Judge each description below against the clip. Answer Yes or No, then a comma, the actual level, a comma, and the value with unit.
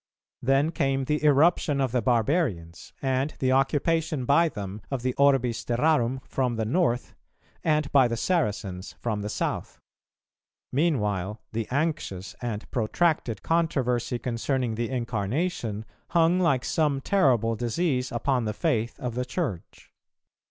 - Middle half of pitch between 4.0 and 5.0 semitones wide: Yes, average, 4.7 semitones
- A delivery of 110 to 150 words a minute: Yes, slow, 135 wpm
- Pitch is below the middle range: Yes, low, 130 Hz